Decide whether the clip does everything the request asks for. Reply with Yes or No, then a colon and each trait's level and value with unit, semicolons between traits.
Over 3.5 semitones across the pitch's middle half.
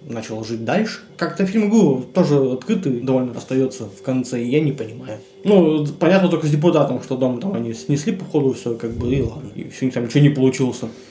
Yes: wide, 5.5 semitones